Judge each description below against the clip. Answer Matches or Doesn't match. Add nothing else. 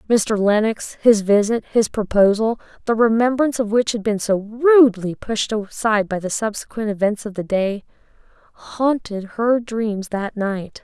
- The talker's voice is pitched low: Doesn't match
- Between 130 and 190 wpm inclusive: Matches